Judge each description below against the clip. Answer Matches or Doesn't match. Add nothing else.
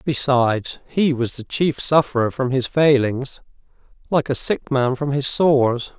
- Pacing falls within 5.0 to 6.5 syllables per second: Doesn't match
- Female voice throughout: Doesn't match